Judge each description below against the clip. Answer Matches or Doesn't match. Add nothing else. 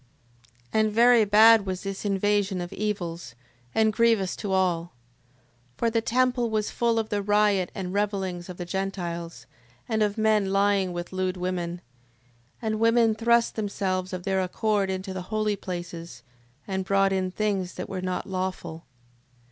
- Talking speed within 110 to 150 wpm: Doesn't match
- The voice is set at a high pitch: Matches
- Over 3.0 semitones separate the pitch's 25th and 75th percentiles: Doesn't match